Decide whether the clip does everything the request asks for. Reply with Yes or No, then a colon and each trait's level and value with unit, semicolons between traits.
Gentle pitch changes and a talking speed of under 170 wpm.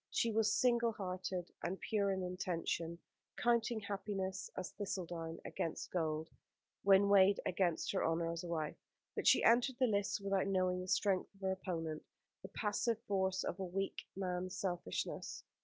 Yes: narrow, 2.3 semitones; average, 160 wpm